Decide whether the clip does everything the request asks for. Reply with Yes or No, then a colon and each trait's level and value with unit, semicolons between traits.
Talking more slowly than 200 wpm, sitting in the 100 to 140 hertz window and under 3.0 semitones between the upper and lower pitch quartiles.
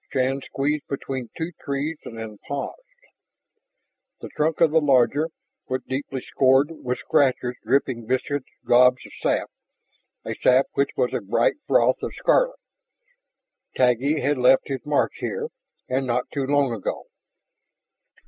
Yes: average, 140 wpm; low, 135 Hz; narrow, 2.4 semitones